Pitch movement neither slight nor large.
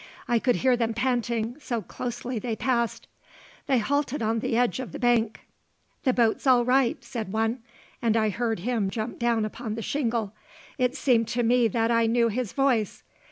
No: narrow, 1.8 semitones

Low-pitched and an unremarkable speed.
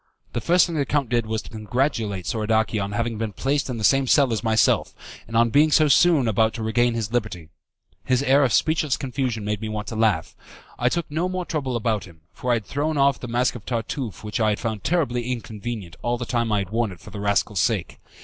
No: low, 115 Hz; fast, 240 wpm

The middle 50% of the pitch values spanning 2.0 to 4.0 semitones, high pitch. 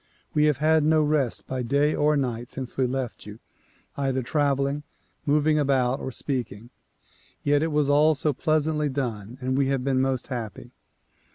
No: average, 2.8 semitones; medium, 140 Hz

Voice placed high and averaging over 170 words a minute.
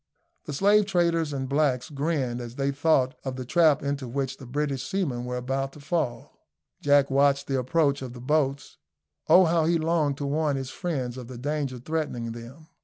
No: medium, 140 Hz; average, 190 wpm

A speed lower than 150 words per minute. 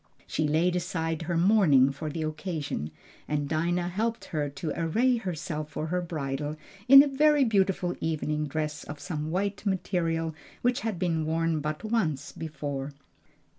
No: average, 155 wpm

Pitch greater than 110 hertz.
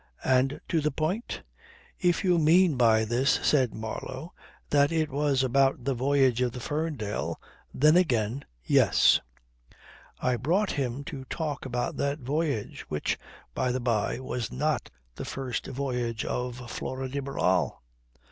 Yes: low, 135 Hz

